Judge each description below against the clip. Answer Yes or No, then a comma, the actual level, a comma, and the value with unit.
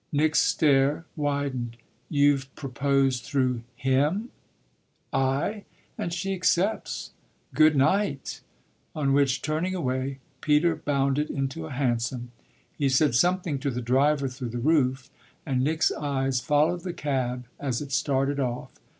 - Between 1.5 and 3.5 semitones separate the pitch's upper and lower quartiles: Yes, average, 2.8 semitones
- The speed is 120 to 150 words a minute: Yes, slow, 135 wpm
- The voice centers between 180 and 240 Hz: No, medium, 140 Hz